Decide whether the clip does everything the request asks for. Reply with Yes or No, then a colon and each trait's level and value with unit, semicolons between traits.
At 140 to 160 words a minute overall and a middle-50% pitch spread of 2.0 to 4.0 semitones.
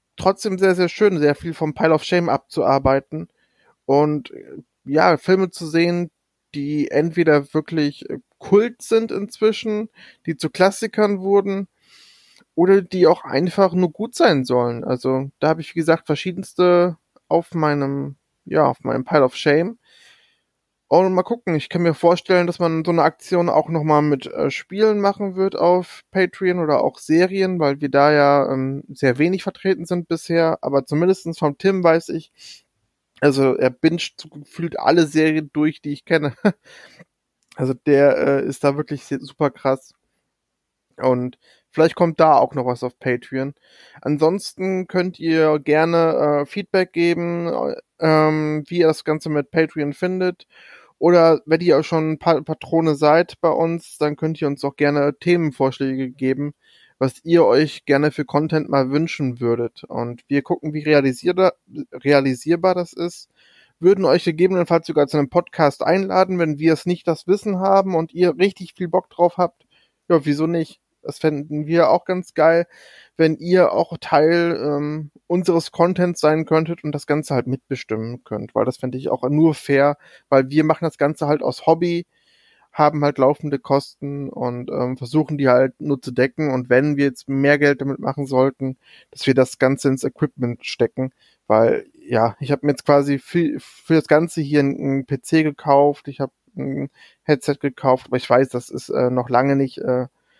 No: average, 170 wpm; average, 3.7 semitones